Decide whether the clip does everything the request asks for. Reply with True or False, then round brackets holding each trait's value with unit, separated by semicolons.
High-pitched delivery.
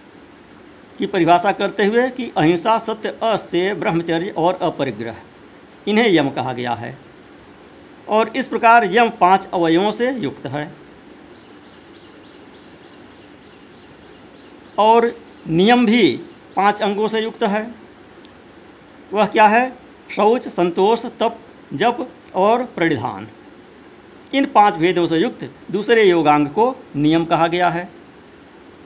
True (205 Hz)